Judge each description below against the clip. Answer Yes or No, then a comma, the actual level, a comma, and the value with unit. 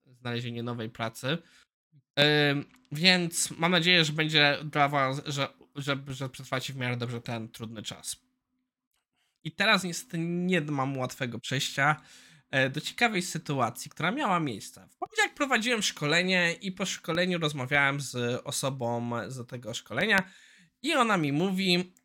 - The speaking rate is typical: Yes, average, 140 wpm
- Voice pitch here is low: No, medium, 150 Hz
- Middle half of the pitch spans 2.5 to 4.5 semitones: No, wide, 5.4 semitones